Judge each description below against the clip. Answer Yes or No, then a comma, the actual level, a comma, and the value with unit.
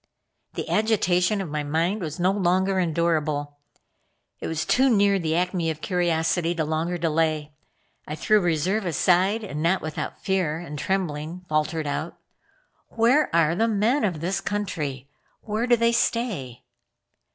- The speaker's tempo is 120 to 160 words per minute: Yes, average, 150 wpm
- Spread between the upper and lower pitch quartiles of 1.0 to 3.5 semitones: No, average, 4.2 semitones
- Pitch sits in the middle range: Yes, medium, 175 Hz